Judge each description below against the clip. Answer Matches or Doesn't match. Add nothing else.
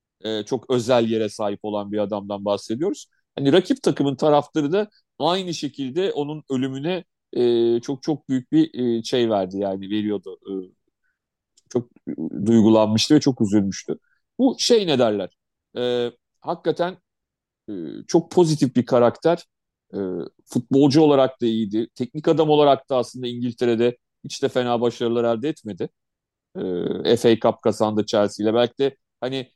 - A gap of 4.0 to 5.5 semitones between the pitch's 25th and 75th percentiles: Matches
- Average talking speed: Matches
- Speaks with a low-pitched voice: Matches